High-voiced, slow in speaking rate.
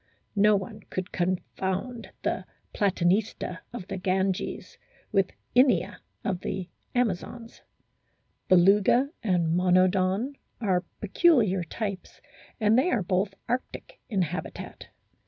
Yes: high, 195 Hz; slow, 105 wpm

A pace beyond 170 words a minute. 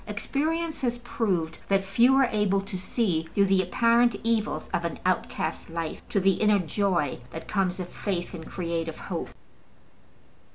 No: average, 160 wpm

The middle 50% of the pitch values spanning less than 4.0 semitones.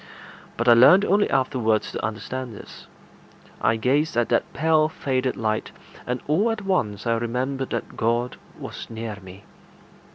No: average, 4.7 semitones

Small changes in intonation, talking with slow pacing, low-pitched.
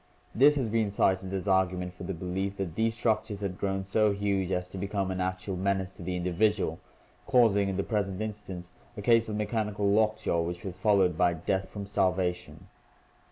No: narrow, 2.3 semitones; average, 190 wpm; very low, 95 Hz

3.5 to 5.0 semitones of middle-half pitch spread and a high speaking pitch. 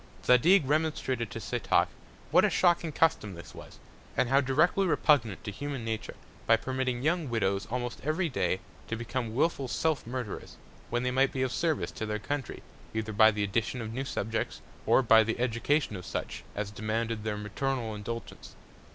No: average, 4.0 semitones; low, 120 Hz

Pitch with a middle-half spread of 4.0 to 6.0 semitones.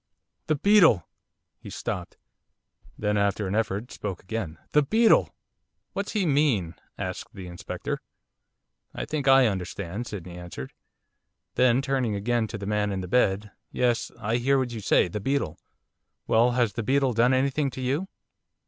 Yes: average, 5.3 semitones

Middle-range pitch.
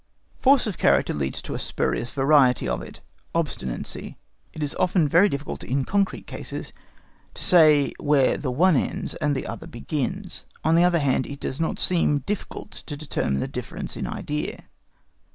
Yes: medium, 150 Hz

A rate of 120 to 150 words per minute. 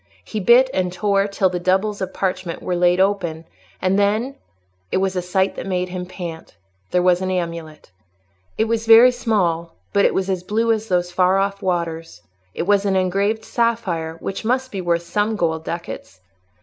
No: average, 180 wpm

